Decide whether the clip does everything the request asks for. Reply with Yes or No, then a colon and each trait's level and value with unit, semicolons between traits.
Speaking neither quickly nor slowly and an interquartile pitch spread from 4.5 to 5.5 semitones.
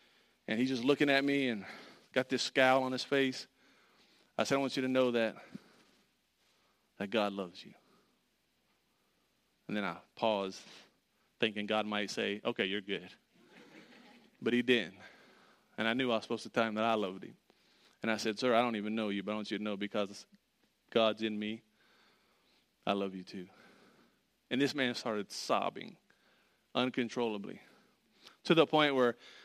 No: average, 175 wpm; average, 3.7 semitones